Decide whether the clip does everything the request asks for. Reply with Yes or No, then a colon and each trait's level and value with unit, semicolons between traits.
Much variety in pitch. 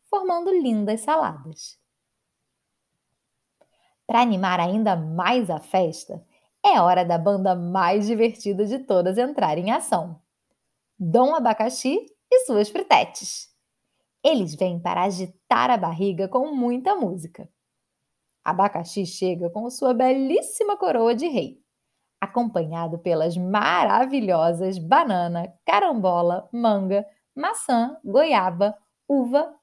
Yes: wide, 5.9 semitones